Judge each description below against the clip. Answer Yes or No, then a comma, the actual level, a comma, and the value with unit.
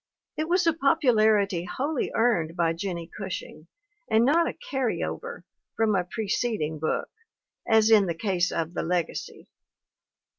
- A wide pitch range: Yes, wide, 6.6 semitones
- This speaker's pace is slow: No, average, 145 wpm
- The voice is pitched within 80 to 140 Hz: No, high, 215 Hz